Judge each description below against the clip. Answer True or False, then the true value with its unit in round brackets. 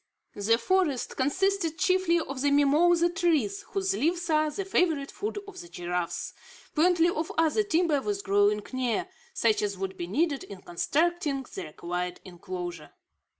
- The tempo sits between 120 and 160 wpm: True (150 wpm)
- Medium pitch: False (290 Hz)